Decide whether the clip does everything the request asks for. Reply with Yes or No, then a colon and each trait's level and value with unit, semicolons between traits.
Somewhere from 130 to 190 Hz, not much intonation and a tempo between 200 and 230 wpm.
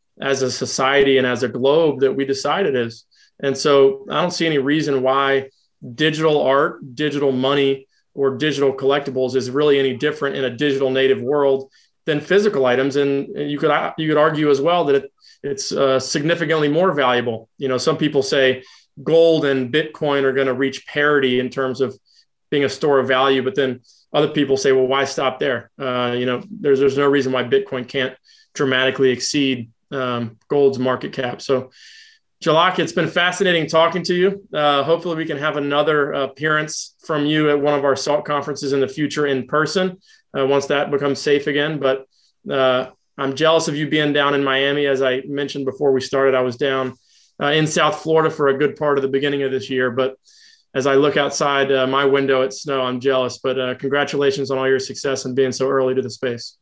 Yes: medium, 140 Hz; narrow, 2.3 semitones; fast, 205 wpm